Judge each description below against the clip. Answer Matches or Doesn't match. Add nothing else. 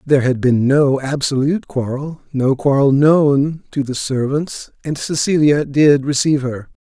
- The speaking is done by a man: Matches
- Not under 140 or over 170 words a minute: Matches